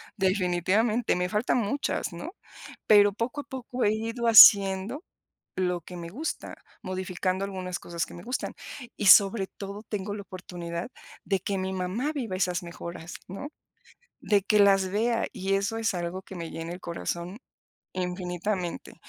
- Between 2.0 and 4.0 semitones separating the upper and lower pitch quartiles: Yes, average, 3.1 semitones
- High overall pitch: Yes, high, 195 Hz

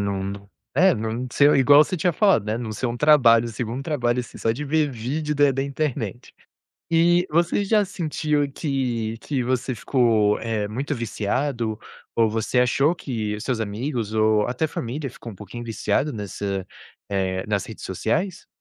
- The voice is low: Yes, low, 120 Hz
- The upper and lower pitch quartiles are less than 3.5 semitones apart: No, average, 5.1 semitones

